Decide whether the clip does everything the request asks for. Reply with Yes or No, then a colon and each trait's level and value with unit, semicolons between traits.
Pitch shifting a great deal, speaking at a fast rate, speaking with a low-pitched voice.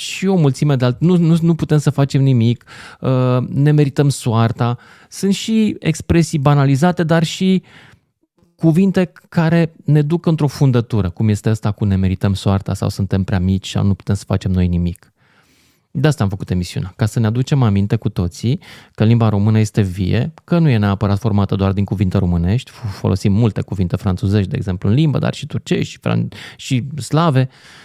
Yes: wide, 6.9 semitones; fast, 185 wpm; low, 120 Hz